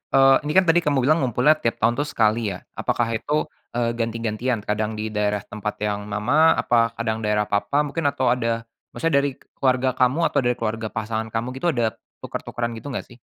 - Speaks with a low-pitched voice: Yes, low, 115 Hz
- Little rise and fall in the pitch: No, average, 3.3 semitones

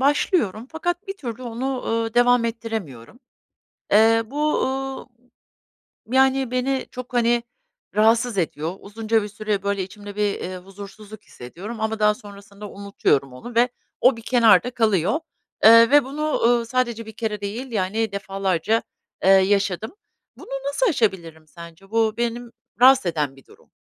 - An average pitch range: Yes, average, 3.6 semitones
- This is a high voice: Yes, high, 220 Hz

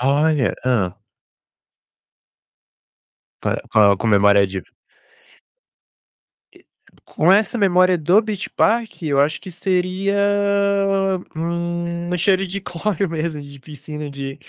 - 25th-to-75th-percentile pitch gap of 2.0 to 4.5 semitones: No, average, 4.9 semitones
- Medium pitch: Yes, medium, 165 Hz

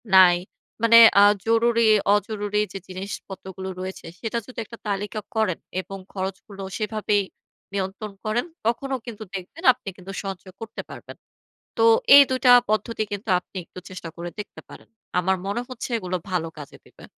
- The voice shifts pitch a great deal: No, average, 3.0 semitones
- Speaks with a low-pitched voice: No, high, 205 Hz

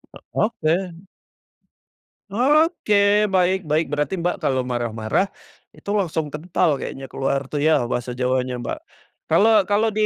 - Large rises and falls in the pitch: Yes, wide, 7.0 semitones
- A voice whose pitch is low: No, medium, 165 Hz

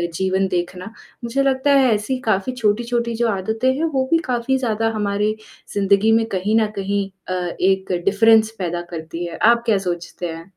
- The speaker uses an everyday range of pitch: Yes, average, 3.7 semitones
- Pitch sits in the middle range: No, high, 215 Hz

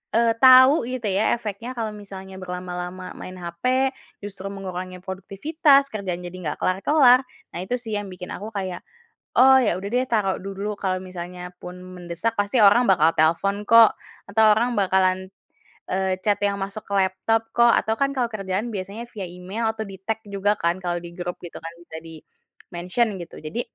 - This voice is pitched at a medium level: No, high, 195 Hz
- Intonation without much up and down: No, average, 3.6 semitones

